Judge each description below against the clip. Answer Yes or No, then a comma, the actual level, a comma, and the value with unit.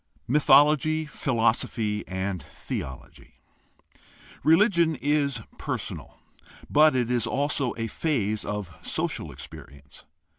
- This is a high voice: No, low, 125 Hz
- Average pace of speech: No, slow, 105 wpm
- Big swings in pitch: Yes, wide, 6.3 semitones